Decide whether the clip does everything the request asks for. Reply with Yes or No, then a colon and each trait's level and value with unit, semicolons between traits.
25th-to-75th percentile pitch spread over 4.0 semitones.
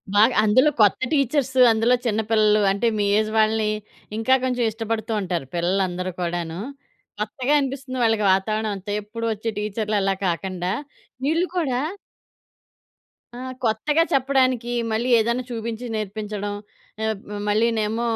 No: average, 3.1 semitones